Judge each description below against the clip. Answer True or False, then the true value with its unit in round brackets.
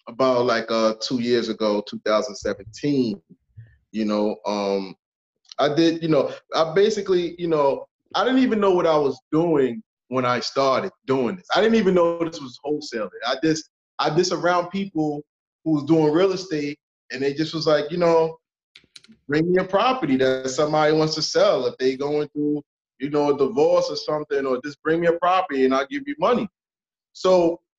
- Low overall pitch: False (150 Hz)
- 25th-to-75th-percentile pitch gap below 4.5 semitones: False (4.8 semitones)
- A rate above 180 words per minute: True (190 wpm)